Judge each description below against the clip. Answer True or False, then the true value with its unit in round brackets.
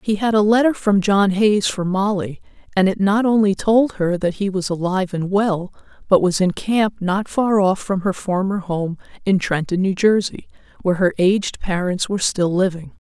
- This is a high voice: True (195 Hz)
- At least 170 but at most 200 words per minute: True (195 wpm)